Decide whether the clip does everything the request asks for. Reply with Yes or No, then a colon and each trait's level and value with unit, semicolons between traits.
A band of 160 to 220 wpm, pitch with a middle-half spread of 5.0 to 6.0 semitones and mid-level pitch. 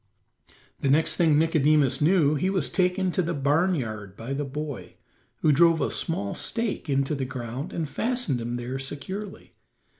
No: average, 170 wpm; average, 4.3 semitones; medium, 150 Hz